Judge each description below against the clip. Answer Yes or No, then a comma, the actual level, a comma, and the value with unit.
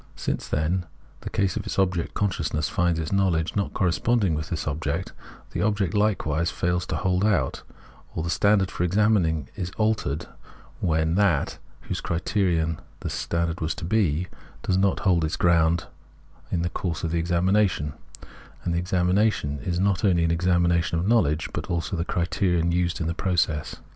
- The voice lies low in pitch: Yes, very low, 85 Hz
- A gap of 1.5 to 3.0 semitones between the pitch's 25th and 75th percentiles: Yes, average, 2.7 semitones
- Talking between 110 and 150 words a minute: No, average, 175 wpm